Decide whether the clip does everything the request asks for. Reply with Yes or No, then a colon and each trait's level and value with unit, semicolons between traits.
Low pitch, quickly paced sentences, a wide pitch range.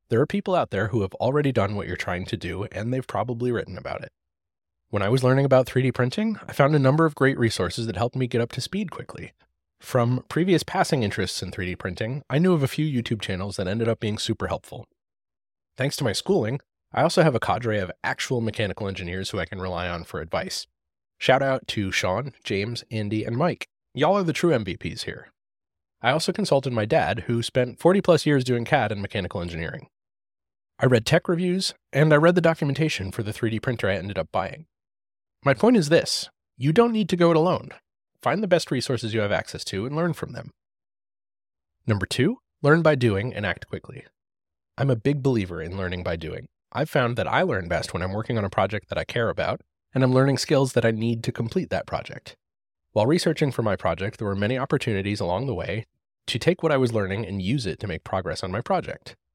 Yes: low, 120 Hz; fast, 225 wpm; wide, 6.0 semitones